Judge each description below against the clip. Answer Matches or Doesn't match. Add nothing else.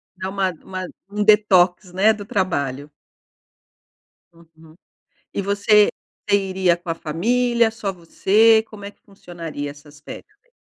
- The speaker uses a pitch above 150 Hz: Matches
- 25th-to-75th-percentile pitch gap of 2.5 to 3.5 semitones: Doesn't match